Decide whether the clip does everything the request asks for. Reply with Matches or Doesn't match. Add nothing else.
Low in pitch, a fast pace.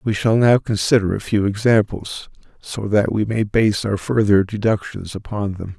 Doesn't match